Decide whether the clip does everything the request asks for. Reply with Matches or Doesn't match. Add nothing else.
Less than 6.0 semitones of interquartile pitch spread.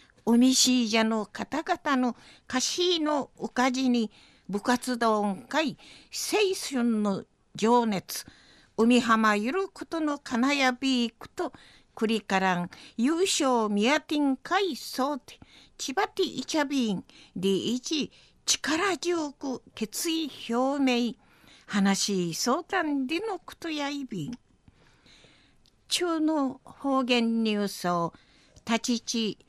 Matches